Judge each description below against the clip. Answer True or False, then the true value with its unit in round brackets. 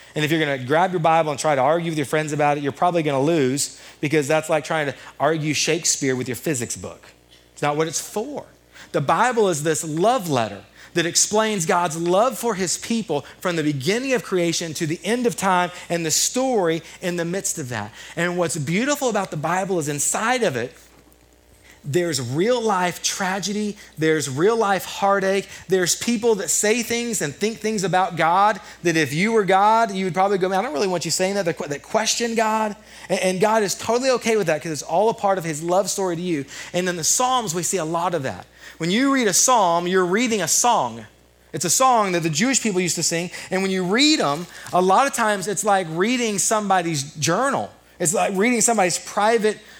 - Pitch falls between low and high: True (180 Hz)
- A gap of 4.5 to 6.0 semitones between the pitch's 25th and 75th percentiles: True (5.0 semitones)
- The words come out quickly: True (220 wpm)